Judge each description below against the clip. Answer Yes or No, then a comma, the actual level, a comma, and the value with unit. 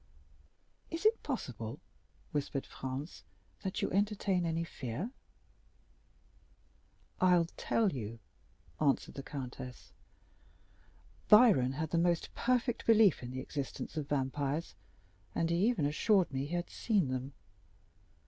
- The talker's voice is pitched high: No, medium, 165 Hz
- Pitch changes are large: Yes, wide, 6.6 semitones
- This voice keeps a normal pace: No, slow, 120 wpm